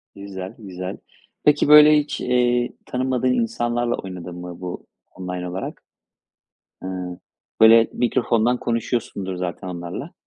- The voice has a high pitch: No, low, 110 Hz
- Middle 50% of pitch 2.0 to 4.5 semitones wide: No, average, 5.2 semitones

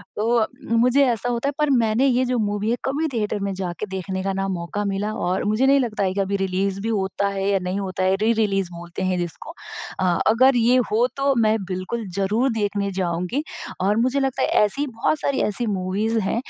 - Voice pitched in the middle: No, high, 210 Hz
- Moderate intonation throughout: Yes, average, 3.9 semitones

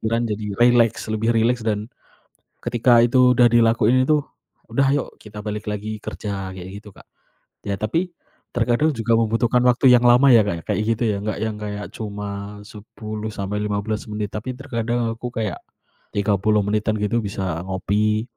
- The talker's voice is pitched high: No, low, 110 Hz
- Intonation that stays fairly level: Yes, narrow, 2.3 semitones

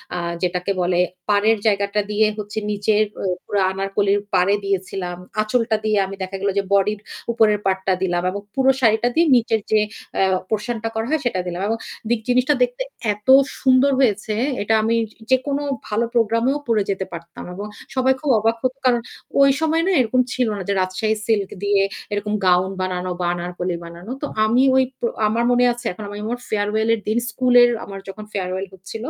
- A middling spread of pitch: Yes, average, 3.4 semitones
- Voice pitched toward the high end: Yes, high, 210 Hz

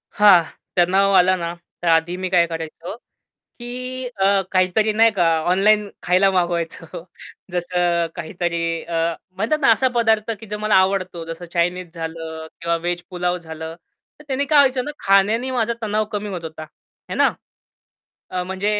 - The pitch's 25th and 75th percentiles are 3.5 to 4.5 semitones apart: Yes, average, 3.9 semitones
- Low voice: No, medium, 185 Hz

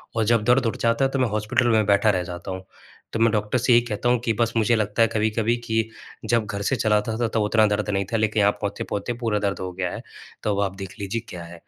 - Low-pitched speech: Yes, low, 110 Hz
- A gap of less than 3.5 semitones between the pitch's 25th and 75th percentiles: Yes, narrow, 2.4 semitones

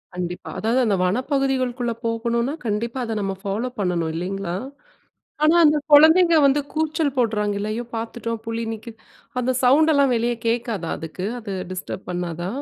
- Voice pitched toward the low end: No, high, 230 Hz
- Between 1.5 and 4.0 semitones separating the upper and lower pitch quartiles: No, average, 4.6 semitones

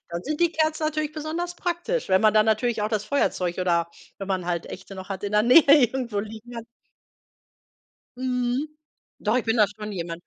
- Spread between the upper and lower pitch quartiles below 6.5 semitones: No, wide, 6.9 semitones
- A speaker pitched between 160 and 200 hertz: No, high, 220 Hz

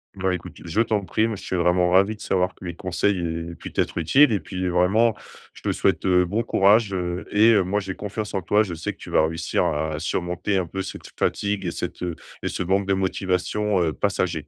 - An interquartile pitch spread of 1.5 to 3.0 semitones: Yes, average, 2.7 semitones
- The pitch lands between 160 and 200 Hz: No, very low, 95 Hz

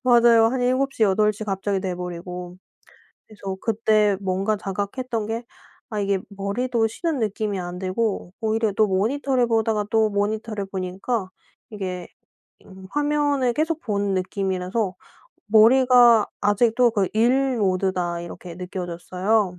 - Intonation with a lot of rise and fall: No, average, 3.6 semitones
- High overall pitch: Yes, high, 210 Hz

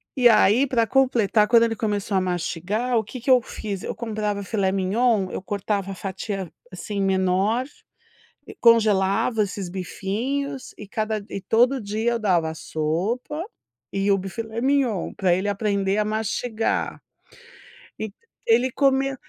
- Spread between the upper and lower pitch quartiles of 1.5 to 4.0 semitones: Yes, average, 3.4 semitones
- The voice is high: Yes, high, 210 Hz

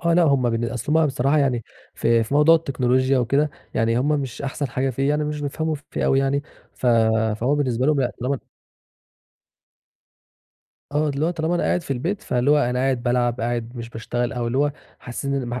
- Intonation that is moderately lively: Yes, average, 3.3 semitones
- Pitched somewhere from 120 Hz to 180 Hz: Yes, low, 135 Hz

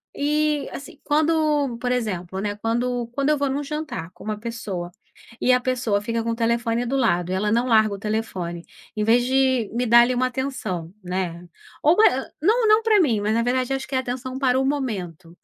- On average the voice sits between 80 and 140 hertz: No, high, 240 Hz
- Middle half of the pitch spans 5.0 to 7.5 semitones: No, average, 4.3 semitones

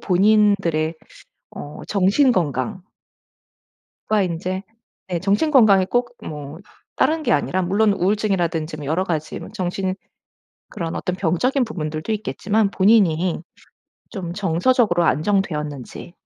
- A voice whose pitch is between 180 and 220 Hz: Yes, medium, 185 Hz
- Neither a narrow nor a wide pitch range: Yes, average, 4.3 semitones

